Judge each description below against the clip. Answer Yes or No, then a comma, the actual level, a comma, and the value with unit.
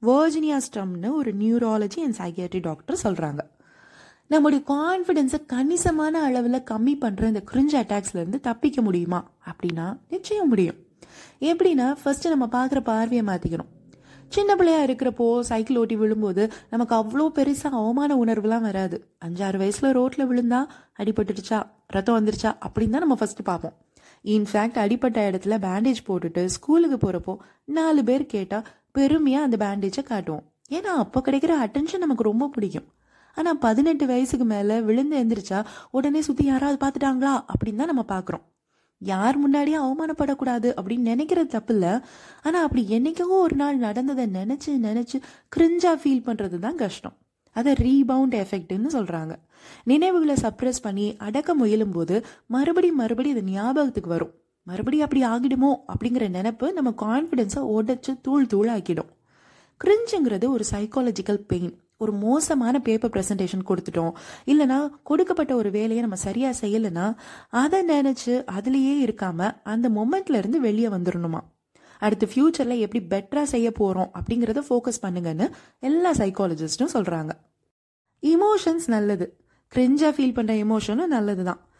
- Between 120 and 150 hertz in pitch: No, high, 240 Hz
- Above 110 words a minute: Yes, average, 120 wpm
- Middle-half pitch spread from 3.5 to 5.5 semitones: Yes, average, 5.2 semitones